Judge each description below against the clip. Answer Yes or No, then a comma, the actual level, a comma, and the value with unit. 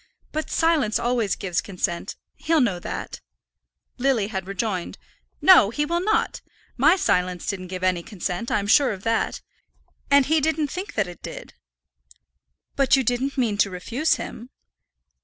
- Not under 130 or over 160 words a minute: Yes, average, 155 wpm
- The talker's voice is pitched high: Yes, high, 235 Hz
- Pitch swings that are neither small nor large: No, wide, 7.4 semitones